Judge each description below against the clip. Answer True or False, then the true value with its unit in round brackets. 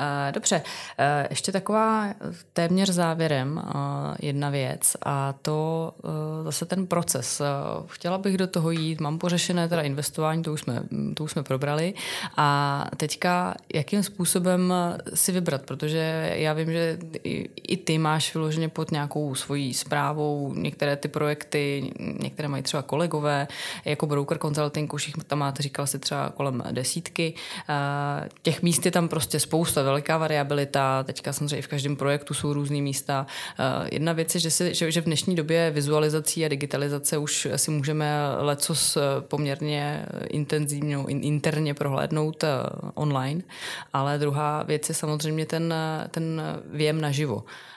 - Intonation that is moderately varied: False (2.2 semitones)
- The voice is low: False (150 Hz)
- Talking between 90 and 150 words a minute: True (140 wpm)